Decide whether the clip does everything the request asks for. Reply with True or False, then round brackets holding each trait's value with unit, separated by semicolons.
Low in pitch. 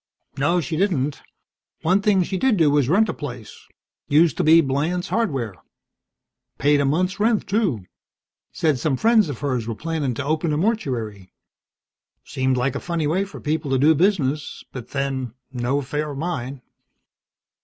False (150 Hz)